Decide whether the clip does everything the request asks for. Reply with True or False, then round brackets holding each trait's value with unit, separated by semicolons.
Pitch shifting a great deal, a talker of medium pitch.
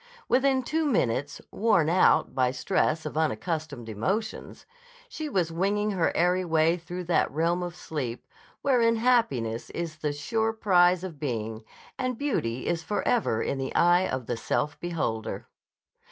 True (6.5 semitones; 170 Hz)